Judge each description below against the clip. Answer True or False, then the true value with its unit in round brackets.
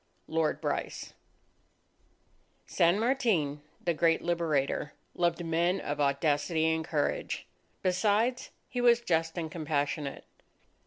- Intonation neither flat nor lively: True (3.4 semitones)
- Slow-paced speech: True (110 wpm)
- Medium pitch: True (165 Hz)